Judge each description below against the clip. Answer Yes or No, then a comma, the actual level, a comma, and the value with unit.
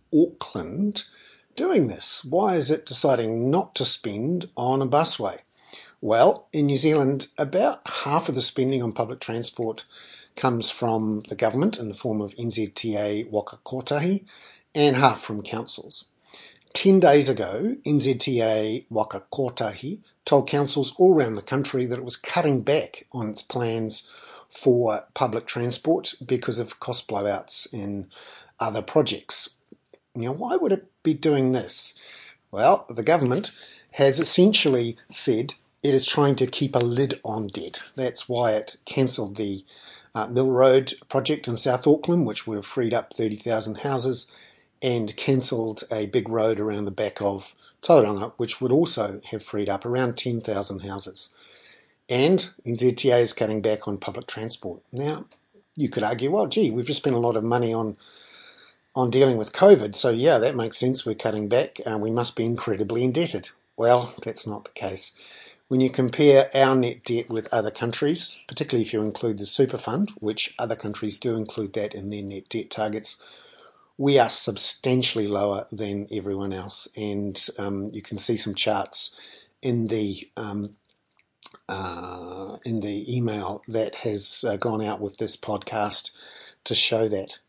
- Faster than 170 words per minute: No, average, 160 wpm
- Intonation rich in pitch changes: No, average, 3.9 semitones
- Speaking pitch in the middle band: No, low, 115 Hz